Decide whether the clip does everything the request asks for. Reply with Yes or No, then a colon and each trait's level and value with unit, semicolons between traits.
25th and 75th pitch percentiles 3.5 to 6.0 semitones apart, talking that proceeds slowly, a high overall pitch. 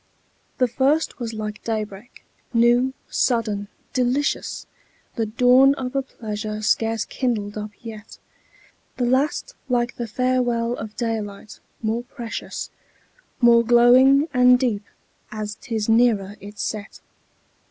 No: average, 2.7 semitones; slow, 120 wpm; high, 235 Hz